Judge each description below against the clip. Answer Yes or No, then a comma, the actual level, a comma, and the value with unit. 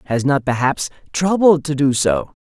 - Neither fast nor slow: Yes, average, 170 wpm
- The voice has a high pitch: No, medium, 140 Hz